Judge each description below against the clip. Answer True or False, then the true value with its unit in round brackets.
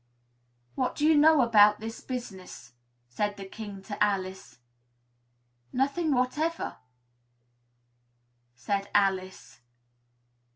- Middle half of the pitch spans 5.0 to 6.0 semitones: True (5.5 semitones)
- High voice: True (215 Hz)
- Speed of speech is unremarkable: False (90 wpm)